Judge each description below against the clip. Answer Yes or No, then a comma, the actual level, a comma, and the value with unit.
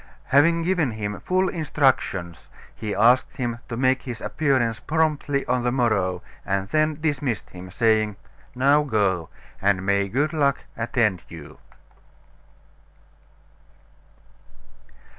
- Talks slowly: Yes, slow, 115 wpm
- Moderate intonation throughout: No, wide, 6.2 semitones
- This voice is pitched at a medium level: No, low, 120 Hz